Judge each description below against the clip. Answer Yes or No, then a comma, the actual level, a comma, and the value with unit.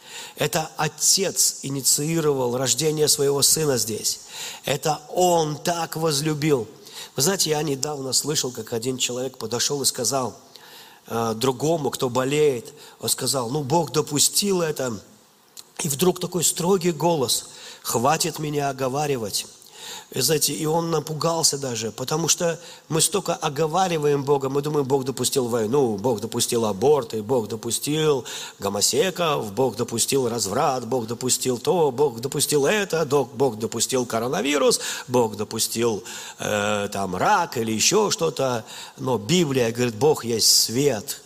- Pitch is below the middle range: No, medium, 145 Hz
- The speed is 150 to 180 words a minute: No, average, 130 wpm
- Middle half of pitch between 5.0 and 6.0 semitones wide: No, average, 4.1 semitones